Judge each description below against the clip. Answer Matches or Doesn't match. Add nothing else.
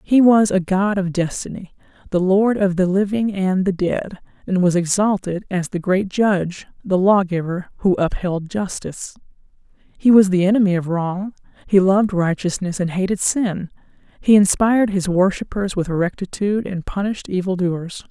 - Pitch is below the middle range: Doesn't match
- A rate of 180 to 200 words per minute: Doesn't match